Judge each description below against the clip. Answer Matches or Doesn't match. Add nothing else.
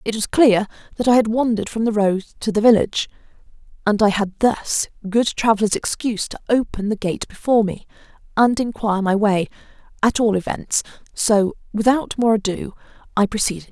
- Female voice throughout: Matches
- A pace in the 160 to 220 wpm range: Matches